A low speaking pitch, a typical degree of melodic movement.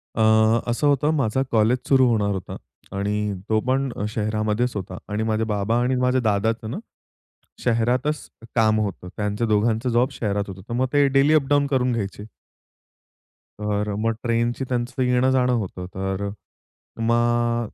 Yes: low, 115 Hz; average, 3.2 semitones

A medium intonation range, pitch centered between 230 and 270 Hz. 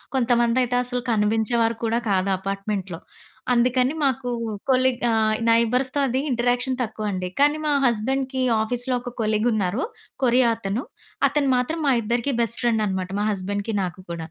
Yes: average, 3.2 semitones; high, 235 Hz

